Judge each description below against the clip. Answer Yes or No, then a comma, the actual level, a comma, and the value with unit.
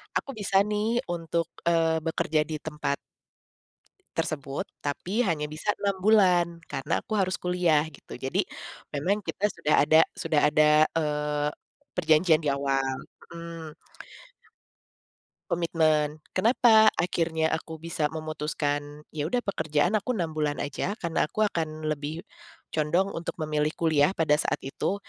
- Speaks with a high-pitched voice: No, medium, 160 Hz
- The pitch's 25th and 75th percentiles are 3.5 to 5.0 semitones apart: No, average, 2.8 semitones